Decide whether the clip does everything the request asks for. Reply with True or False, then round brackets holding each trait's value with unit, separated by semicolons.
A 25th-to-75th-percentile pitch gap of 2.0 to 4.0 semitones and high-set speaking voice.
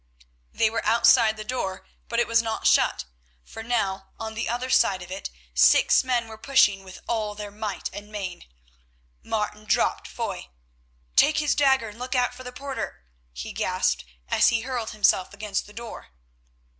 True (2.9 semitones; 220 Hz)